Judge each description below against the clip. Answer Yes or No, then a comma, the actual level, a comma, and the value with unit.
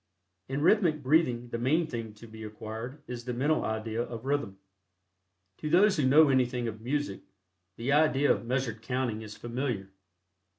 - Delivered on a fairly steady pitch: No, average, 4.2 semitones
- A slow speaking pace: No, average, 165 wpm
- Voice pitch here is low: Yes, low, 125 Hz